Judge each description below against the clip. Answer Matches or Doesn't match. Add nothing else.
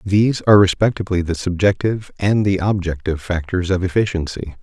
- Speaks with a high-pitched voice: Doesn't match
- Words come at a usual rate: Matches